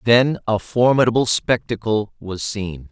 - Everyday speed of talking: No, slow, 125 wpm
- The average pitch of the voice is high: No, low, 110 Hz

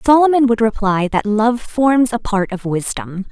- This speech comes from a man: No, female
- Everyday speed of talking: Yes, average, 180 wpm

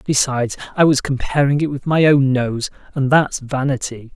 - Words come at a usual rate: Yes, average, 175 wpm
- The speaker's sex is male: Yes, male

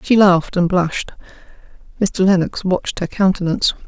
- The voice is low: No, medium, 185 Hz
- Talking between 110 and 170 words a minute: Yes, average, 140 wpm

